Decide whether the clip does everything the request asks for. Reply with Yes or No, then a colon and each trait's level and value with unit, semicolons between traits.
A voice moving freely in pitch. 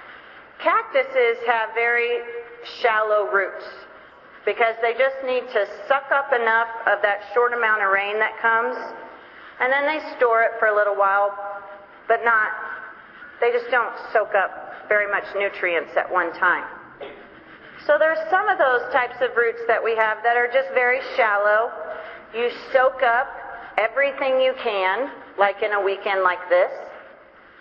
No: average, 3.9 semitones